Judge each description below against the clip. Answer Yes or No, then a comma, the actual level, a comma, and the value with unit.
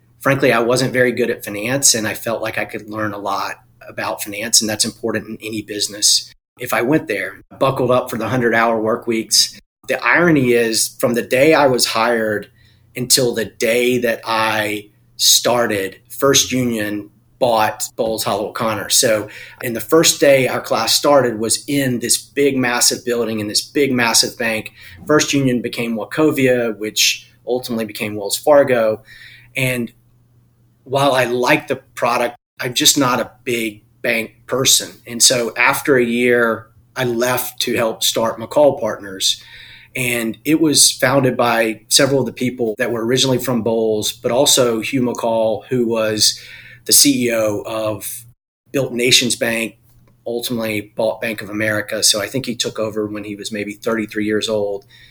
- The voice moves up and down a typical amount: No, narrow, 2.3 semitones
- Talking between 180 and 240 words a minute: No, average, 165 wpm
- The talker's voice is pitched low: Yes, low, 115 Hz